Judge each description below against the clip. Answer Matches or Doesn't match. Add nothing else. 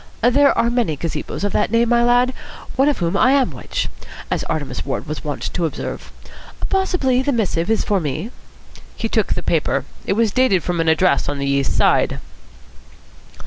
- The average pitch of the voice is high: Matches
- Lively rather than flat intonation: Matches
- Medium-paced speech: Matches